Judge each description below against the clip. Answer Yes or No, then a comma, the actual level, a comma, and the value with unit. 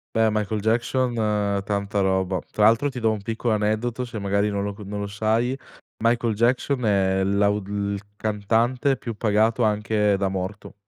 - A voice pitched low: Yes, low, 105 Hz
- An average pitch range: No, narrow, 2.3 semitones